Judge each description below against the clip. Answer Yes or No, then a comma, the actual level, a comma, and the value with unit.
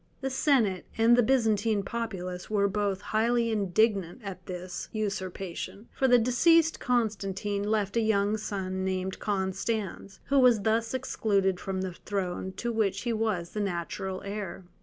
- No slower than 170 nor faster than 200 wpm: No, average, 150 wpm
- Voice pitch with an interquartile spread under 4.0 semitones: Yes, average, 3.1 semitones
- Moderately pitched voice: No, high, 205 Hz